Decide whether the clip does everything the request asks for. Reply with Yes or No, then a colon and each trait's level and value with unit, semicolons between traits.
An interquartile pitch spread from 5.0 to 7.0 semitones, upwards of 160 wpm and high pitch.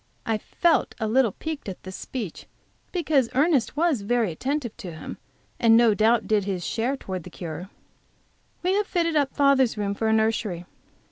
Yes: wide, 5.6 semitones; average, 180 wpm; high, 230 Hz